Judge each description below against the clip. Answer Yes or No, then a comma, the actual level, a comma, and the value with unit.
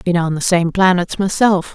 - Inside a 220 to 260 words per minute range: No, fast, 205 wpm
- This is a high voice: No, medium, 180 Hz